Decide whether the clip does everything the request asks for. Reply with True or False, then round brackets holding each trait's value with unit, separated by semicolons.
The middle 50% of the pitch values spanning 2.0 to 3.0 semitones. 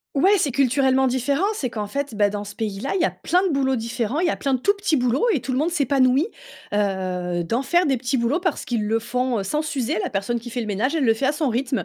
False (4.1 semitones)